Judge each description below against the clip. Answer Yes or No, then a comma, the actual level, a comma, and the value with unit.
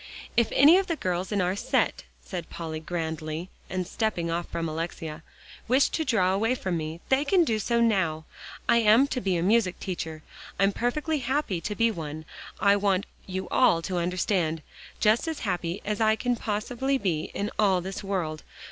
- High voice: Yes, high, 195 Hz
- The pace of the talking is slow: No, average, 185 wpm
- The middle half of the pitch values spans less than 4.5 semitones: No, average, 5.3 semitones